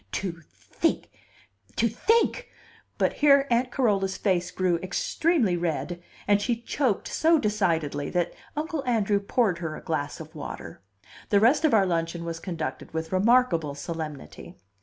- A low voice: No, high, 190 Hz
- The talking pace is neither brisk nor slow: Yes, average, 150 wpm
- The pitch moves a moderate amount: No, wide, 6.2 semitones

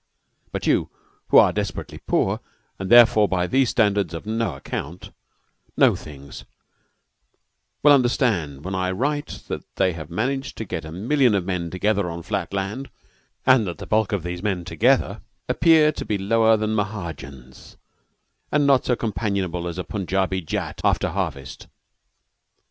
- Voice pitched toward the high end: No, low, 100 Hz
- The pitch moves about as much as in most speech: Yes, average, 4.6 semitones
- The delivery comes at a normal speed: Yes, average, 160 wpm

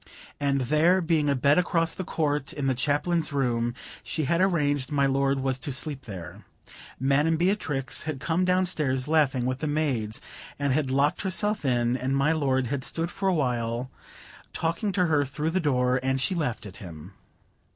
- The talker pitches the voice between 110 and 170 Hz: Yes, medium, 140 Hz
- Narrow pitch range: No, average, 3.9 semitones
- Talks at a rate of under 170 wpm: No, average, 185 wpm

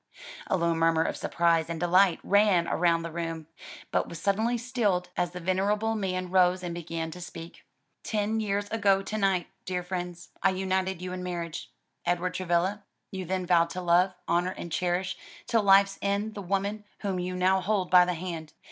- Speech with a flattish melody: Yes, narrow, 2.3 semitones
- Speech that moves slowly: No, average, 185 wpm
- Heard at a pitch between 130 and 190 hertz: Yes, medium, 185 Hz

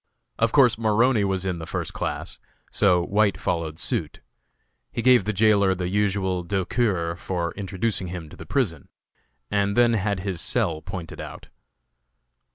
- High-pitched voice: No, very low, 95 Hz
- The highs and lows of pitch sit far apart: No, average, 3.4 semitones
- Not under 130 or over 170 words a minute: Yes, average, 155 wpm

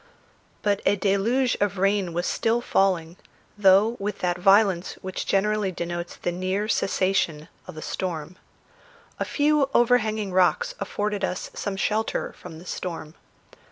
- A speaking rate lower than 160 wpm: Yes, average, 140 wpm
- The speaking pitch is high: Yes, high, 195 Hz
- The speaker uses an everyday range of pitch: Yes, average, 3.0 semitones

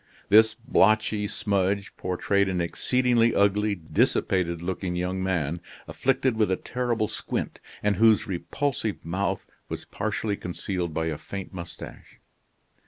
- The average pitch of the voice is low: Yes, low, 100 Hz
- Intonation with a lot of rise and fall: No, average, 3.3 semitones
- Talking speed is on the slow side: Yes, slow, 125 wpm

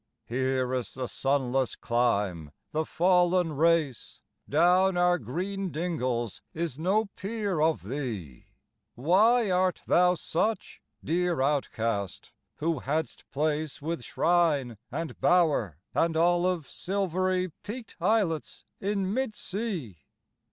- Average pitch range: No, wide, 5.7 semitones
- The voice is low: No, medium, 165 Hz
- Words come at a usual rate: No, slow, 110 wpm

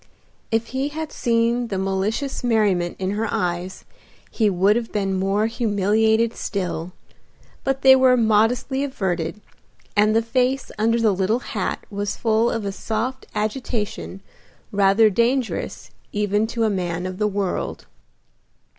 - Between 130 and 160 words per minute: Yes, average, 140 wpm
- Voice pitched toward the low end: No, high, 215 Hz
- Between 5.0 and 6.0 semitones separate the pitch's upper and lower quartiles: No, average, 3.2 semitones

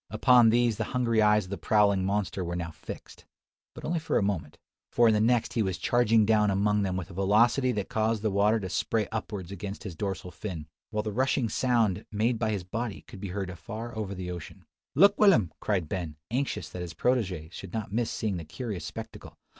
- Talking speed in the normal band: No, fast, 220 wpm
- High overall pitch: No, low, 105 Hz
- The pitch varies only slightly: No, average, 3.4 semitones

